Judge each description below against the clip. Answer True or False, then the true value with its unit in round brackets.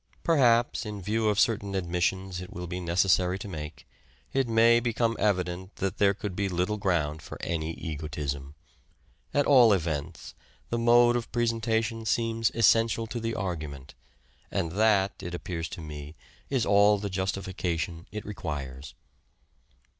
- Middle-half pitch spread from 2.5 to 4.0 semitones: False (5.0 semitones)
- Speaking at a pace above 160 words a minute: False (150 wpm)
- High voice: False (95 Hz)